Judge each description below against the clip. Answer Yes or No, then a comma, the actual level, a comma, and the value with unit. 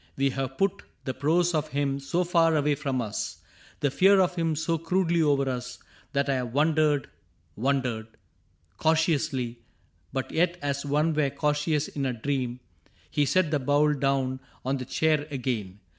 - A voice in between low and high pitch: Yes, medium, 145 Hz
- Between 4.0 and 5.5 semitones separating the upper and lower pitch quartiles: No, average, 3.3 semitones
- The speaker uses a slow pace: No, average, 175 wpm